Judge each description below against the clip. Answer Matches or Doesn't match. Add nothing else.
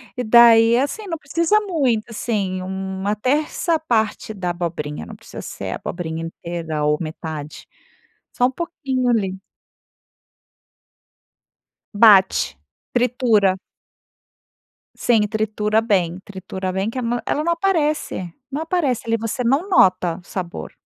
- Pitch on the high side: Matches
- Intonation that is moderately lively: Doesn't match